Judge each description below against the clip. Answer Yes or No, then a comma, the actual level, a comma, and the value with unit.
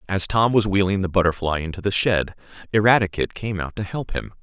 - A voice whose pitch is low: Yes, very low, 95 Hz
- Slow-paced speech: No, fast, 205 wpm